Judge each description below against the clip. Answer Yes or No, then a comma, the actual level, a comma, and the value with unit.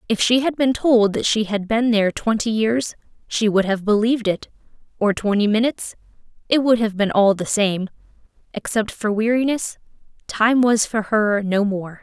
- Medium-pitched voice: No, high, 220 Hz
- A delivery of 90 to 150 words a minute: No, average, 170 wpm